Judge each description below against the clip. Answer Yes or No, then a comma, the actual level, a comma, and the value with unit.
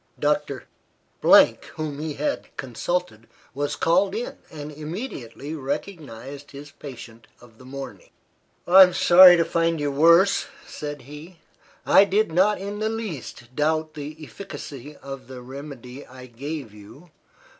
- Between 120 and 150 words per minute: Yes, slow, 135 wpm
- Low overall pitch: No, medium, 150 Hz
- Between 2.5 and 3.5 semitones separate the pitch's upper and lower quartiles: No, average, 4.7 semitones